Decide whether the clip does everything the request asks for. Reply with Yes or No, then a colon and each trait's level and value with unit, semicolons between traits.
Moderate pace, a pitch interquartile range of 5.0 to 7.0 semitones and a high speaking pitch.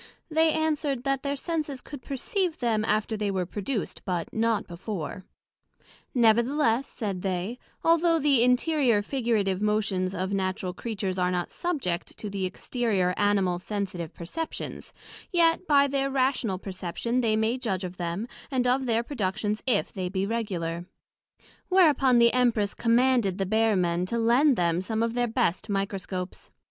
Yes: average, 155 wpm; wide, 5.5 semitones; high, 220 Hz